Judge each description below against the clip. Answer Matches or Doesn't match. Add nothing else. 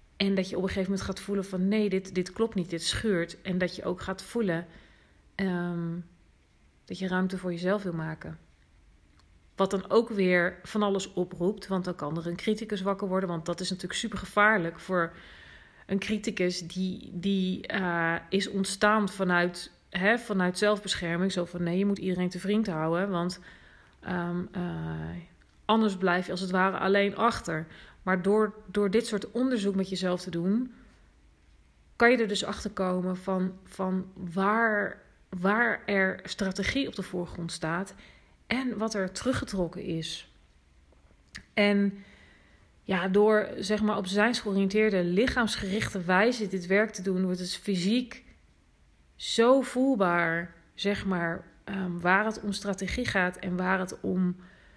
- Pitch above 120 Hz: Matches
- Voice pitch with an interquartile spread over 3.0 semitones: Doesn't match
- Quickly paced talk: Doesn't match